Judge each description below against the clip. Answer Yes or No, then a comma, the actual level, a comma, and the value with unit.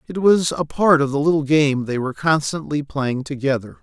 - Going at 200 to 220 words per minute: Yes, fast, 205 wpm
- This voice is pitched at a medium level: Yes, medium, 145 Hz